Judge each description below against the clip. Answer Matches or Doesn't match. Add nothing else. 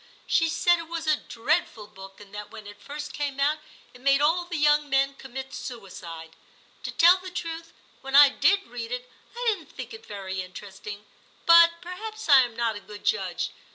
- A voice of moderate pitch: Doesn't match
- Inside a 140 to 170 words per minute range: Doesn't match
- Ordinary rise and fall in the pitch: Doesn't match